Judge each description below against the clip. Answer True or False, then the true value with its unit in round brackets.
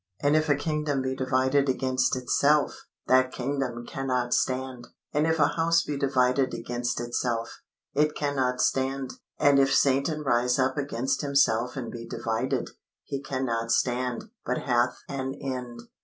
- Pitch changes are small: True (2.2 semitones)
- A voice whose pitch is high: False (130 Hz)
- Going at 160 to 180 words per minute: False (150 wpm)